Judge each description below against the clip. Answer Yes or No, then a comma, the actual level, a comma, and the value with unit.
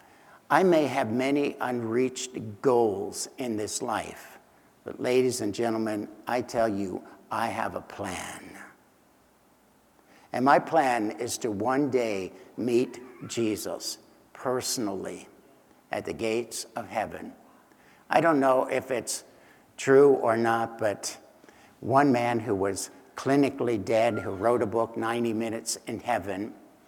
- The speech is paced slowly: Yes, slow, 130 wpm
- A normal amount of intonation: No, narrow, 2.3 semitones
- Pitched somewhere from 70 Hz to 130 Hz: Yes, low, 115 Hz